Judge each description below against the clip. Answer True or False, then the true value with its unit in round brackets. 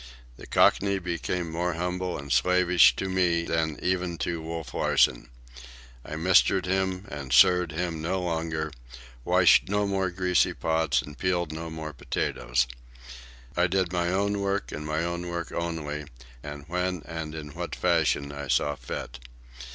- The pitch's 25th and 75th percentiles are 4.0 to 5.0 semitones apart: False (2.7 semitones)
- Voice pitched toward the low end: True (85 Hz)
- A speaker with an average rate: True (155 wpm)